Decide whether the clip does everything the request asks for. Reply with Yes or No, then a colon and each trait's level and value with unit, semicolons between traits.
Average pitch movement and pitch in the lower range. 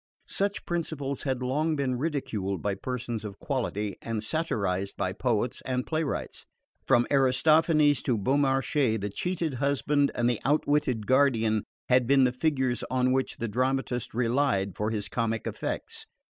Yes: average, 4.1 semitones; low, 130 Hz